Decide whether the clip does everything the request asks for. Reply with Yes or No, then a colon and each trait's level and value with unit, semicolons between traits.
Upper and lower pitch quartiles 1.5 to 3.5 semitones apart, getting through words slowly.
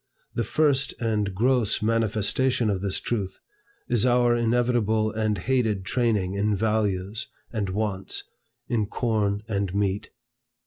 Yes: average, 2.9 semitones; slow, 125 wpm